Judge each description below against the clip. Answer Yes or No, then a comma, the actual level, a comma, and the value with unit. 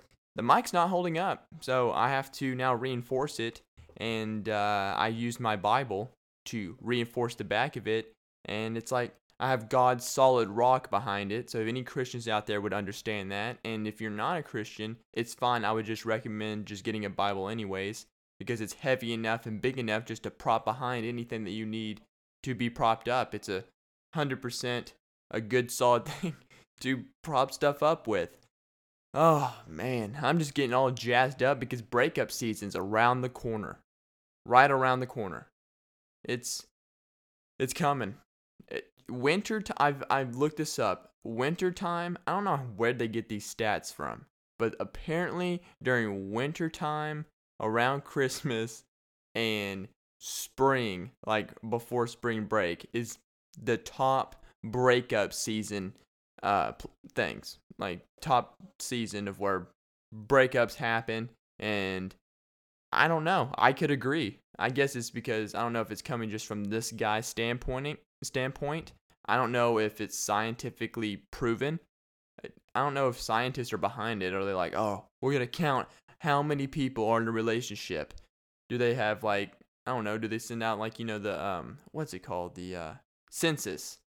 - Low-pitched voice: Yes, low, 115 Hz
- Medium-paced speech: Yes, average, 165 wpm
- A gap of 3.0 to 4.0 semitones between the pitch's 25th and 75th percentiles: Yes, average, 3.5 semitones